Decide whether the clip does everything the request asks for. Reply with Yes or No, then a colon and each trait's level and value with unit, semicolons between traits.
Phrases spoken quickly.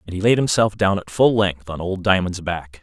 Yes: fast, 255 wpm